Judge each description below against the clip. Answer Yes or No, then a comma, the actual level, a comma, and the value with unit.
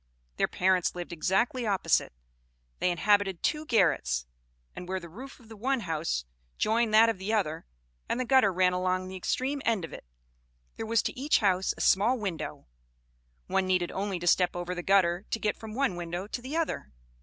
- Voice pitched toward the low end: No, high, 195 Hz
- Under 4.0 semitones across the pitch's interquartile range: No, average, 4.3 semitones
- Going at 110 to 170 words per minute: No, average, 195 wpm